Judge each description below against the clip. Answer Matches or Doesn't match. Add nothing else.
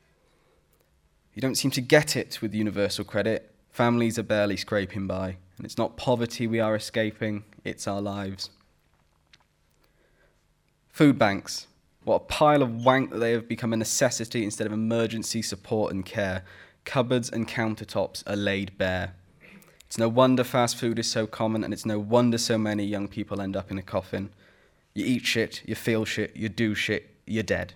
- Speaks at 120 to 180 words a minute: Matches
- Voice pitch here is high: Doesn't match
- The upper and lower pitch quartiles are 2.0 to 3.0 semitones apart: Matches